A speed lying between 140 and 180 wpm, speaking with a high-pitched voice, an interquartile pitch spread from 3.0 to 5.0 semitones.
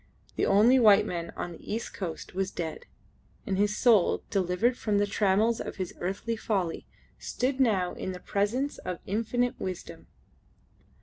Yes: average, 160 wpm; high, 205 Hz; average, 3.8 semitones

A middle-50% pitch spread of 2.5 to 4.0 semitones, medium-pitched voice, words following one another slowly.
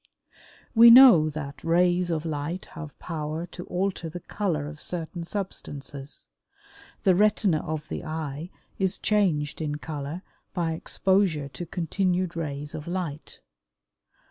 Yes: average, 3.4 semitones; medium, 165 Hz; slow, 130 wpm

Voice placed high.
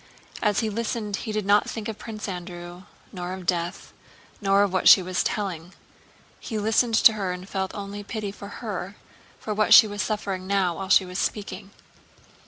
Yes: high, 200 Hz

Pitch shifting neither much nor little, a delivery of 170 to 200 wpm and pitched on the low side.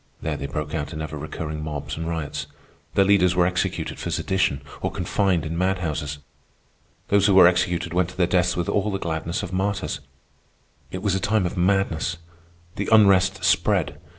Yes: average, 3.3 semitones; average, 180 wpm; very low, 90 Hz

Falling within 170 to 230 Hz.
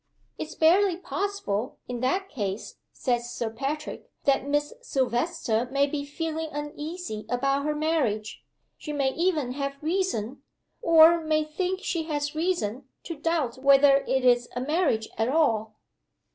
No: very high, 290 Hz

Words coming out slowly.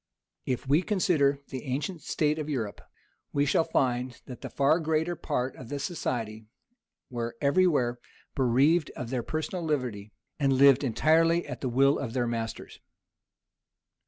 No: average, 155 wpm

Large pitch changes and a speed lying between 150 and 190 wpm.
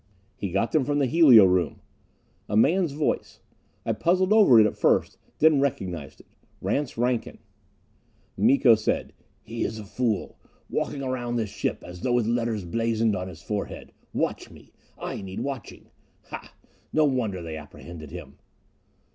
Yes: wide, 5.8 semitones; average, 160 wpm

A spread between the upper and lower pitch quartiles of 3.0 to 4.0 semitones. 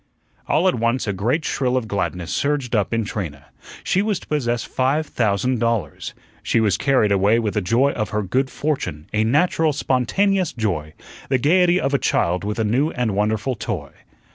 No: average, 5.2 semitones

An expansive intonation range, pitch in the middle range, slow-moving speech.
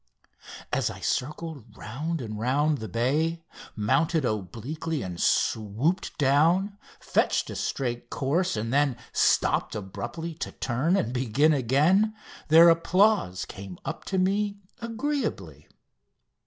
Yes: wide, 6.7 semitones; medium, 145 Hz; slow, 120 wpm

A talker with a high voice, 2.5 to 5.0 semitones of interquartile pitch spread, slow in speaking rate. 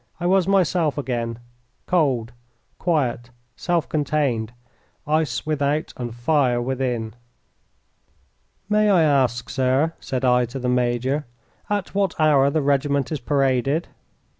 No: medium, 140 Hz; average, 4.0 semitones; slow, 120 wpm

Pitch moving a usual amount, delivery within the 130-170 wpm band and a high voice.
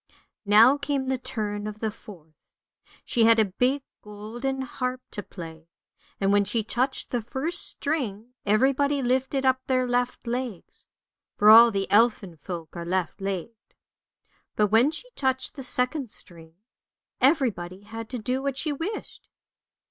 Yes: average, 4.3 semitones; average, 150 wpm; high, 235 Hz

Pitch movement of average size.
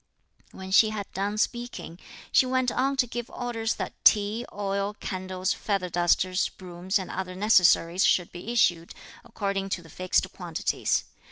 Yes: average, 3.5 semitones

